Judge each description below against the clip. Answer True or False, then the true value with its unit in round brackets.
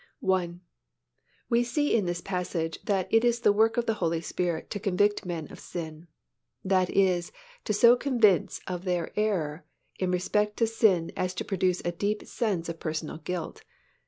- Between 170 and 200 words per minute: True (175 wpm)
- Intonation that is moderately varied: True (3.6 semitones)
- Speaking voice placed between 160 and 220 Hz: True (185 Hz)